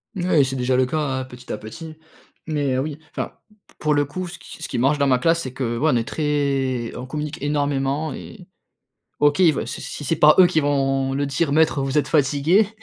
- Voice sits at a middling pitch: Yes, medium, 145 Hz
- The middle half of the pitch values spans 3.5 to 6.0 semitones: No, average, 2.7 semitones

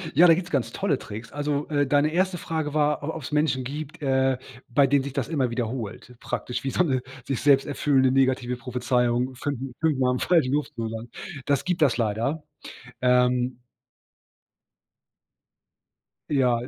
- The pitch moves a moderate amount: Yes, average, 3.1 semitones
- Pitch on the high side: No, low, 135 Hz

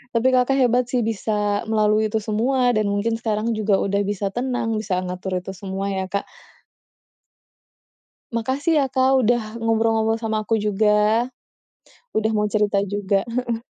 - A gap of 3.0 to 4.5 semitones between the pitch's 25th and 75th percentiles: No, narrow, 2.4 semitones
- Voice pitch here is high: Yes, high, 220 Hz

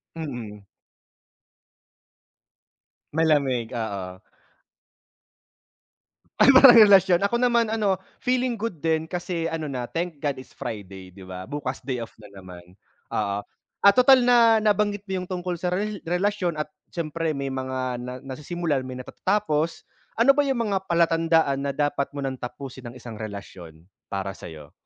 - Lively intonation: Yes, wide, 7.6 semitones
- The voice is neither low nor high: Yes, medium, 155 Hz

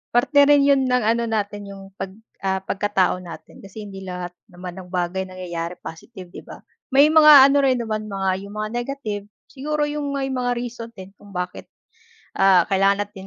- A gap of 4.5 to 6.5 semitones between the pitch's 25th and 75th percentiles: Yes, average, 4.9 semitones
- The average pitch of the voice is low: No, high, 205 Hz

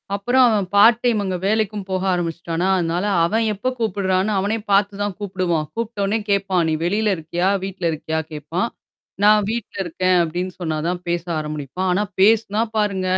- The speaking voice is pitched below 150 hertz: No, high, 190 Hz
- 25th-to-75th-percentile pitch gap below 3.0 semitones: No, average, 3.3 semitones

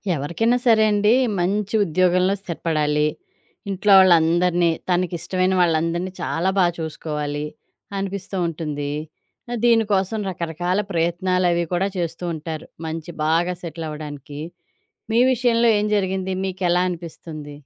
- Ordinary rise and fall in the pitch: Yes, average, 3.0 semitones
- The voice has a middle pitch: Yes, medium, 175 Hz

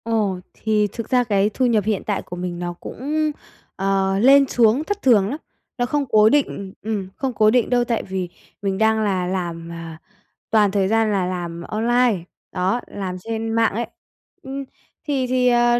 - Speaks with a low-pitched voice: No, high, 215 Hz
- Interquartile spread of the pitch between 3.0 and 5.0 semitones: Yes, average, 4.1 semitones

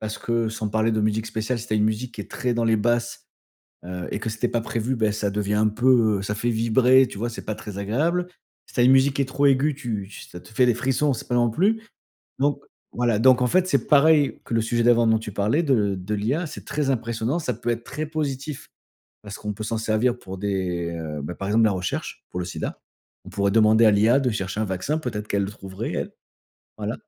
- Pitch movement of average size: Yes, average, 3.6 semitones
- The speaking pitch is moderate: No, low, 115 Hz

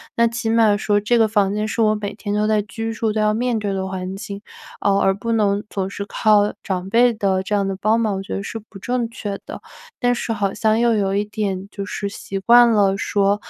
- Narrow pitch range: Yes, narrow, 2.1 semitones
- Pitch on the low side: No, high, 210 Hz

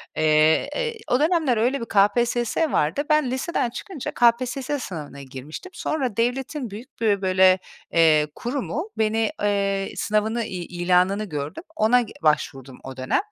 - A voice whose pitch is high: Yes, high, 220 Hz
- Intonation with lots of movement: Yes, wide, 6.5 semitones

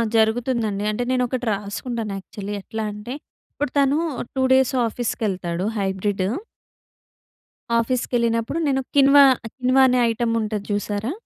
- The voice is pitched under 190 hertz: No, high, 230 Hz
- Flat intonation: No, average, 3.7 semitones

